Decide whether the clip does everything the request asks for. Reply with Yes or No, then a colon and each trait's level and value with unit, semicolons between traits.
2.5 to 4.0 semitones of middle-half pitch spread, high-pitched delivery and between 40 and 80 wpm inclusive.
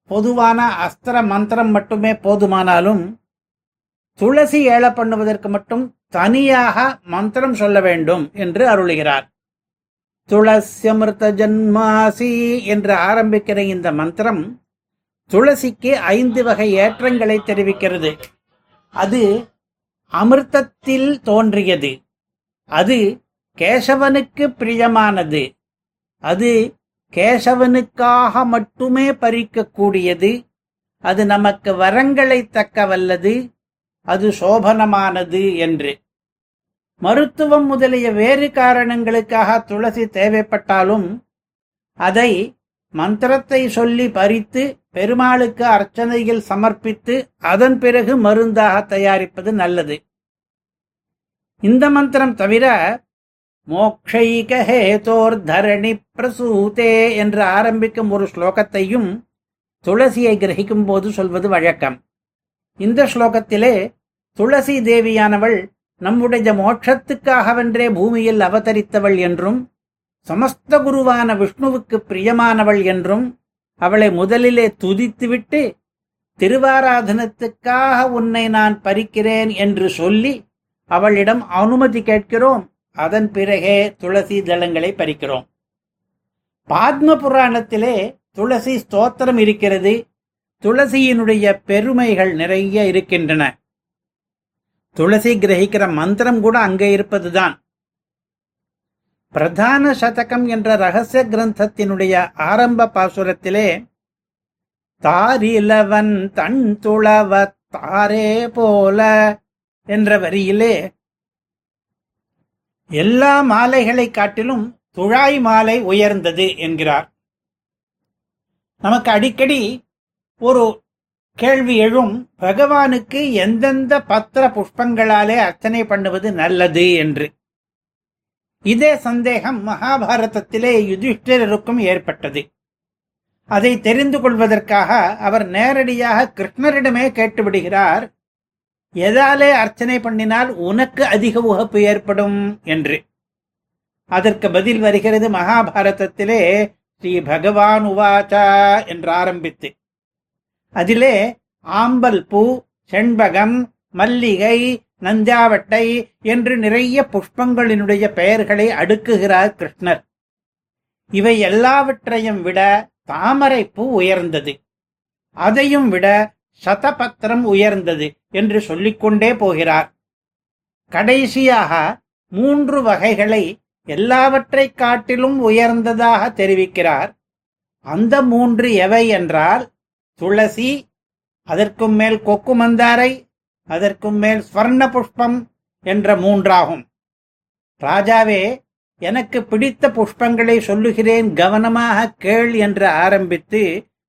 Yes: average, 3.4 semitones; high, 220 Hz; slow, 75 wpm